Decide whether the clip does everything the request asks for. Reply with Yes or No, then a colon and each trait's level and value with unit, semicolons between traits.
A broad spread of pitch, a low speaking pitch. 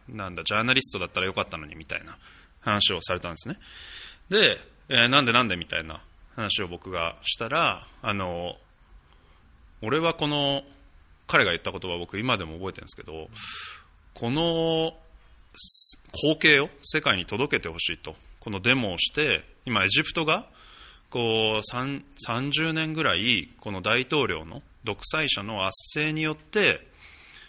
Yes: wide, 7.9 semitones; low, 105 Hz